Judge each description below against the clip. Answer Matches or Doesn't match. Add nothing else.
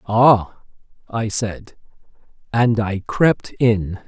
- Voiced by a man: Matches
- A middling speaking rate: Doesn't match